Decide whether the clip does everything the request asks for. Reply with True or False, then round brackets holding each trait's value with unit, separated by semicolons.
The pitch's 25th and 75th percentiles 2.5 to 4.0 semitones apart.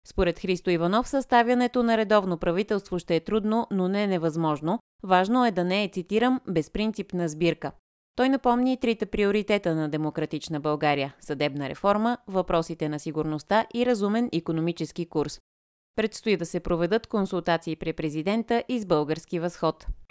False (5.1 semitones)